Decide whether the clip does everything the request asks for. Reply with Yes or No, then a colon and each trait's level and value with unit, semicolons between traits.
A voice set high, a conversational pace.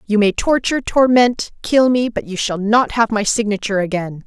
Yes: high, 220 Hz; average, 195 wpm